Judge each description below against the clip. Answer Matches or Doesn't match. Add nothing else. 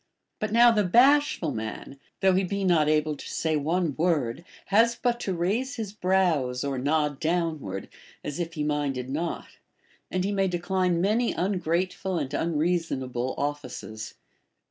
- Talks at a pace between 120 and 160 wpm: Matches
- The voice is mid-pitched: Matches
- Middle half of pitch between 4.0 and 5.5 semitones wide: Matches